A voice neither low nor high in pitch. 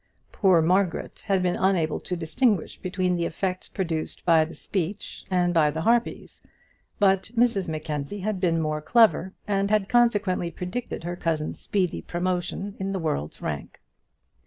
Yes: medium, 180 Hz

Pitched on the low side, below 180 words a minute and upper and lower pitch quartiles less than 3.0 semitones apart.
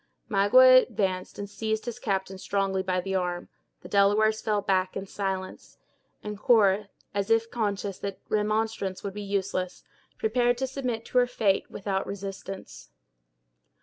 No: high, 200 Hz; average, 150 wpm; narrow, 2.4 semitones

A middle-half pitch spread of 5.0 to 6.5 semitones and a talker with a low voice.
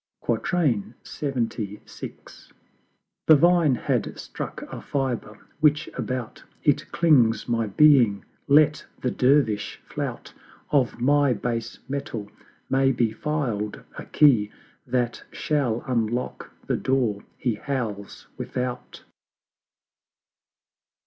No: average, 4.2 semitones; low, 125 Hz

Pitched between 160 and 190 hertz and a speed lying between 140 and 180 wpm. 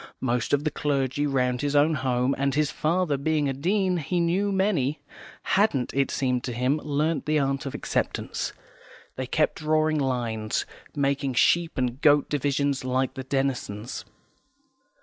No: medium, 140 Hz; average, 155 wpm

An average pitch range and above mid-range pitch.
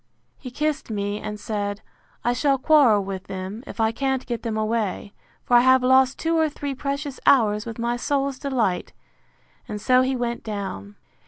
Yes: average, 4.2 semitones; high, 240 Hz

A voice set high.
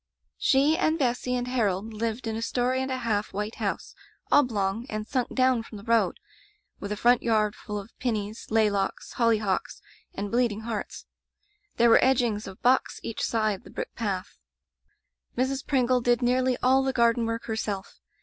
Yes: high, 230 Hz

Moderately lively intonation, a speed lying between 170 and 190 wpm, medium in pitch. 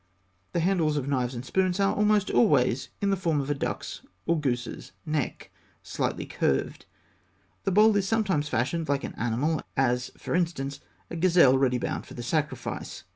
No: wide, 6.0 semitones; average, 180 wpm; medium, 150 Hz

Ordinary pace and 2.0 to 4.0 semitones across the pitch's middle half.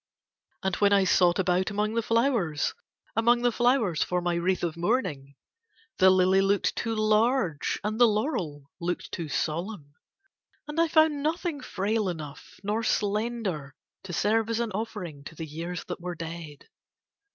No: average, 160 wpm; average, 5.0 semitones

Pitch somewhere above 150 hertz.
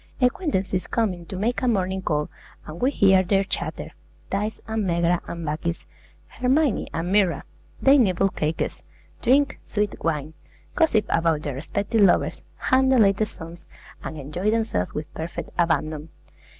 Yes: high, 190 Hz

